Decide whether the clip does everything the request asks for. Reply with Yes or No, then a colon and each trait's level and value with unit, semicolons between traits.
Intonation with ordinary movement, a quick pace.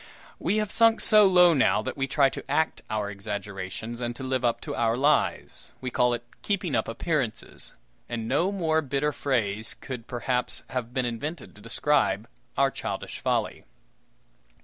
No: average, 4.8 semitones; average, 170 wpm